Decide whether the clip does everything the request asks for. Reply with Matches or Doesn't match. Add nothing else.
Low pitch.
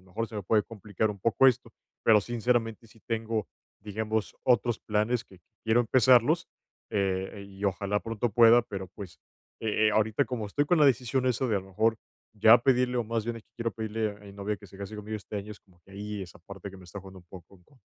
Matches